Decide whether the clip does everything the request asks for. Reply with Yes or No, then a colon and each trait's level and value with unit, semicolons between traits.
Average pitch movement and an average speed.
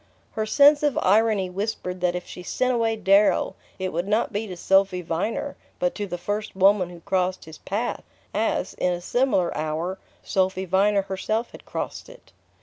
Yes: average, 3.3 semitones; average, 180 wpm